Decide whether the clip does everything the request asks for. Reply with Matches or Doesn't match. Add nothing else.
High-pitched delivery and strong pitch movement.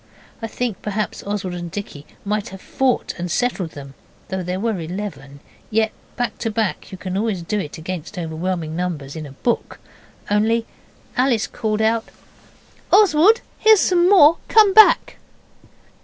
Doesn't match